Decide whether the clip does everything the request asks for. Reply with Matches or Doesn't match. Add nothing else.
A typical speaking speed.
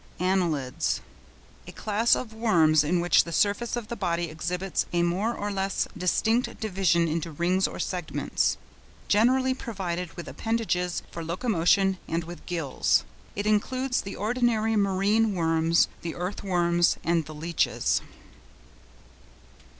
Doesn't match